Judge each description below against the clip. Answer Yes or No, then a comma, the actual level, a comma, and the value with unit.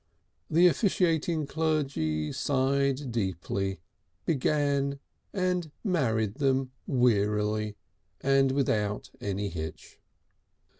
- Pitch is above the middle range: No, low, 135 Hz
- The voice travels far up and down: Yes, wide, 5.9 semitones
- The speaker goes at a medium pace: No, slow, 80 wpm